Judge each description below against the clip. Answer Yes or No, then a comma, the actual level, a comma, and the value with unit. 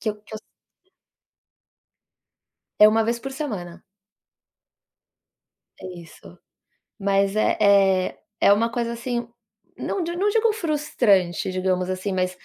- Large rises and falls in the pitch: No, average, 4.4 semitones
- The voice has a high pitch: Yes, high, 210 Hz